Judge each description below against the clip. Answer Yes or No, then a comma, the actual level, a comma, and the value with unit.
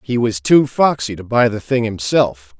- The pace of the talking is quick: Yes, fast, 210 wpm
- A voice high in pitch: No, low, 115 Hz